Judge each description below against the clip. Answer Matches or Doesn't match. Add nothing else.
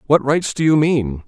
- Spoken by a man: Matches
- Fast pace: Matches